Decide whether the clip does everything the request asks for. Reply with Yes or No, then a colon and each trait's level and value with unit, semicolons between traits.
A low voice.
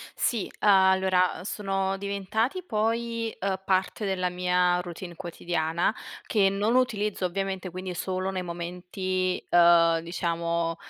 No: medium, 185 Hz